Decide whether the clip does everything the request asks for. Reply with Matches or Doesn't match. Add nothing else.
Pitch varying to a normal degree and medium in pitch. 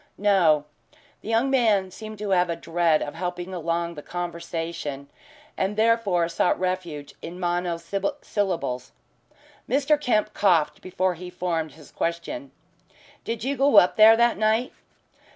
Matches